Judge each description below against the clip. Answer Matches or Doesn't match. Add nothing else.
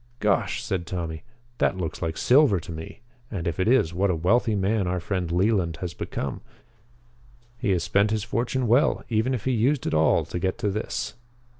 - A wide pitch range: Doesn't match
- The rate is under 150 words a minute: Doesn't match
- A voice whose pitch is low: Matches